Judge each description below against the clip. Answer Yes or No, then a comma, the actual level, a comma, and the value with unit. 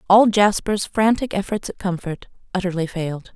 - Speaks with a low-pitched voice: No, high, 195 Hz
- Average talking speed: Yes, average, 145 wpm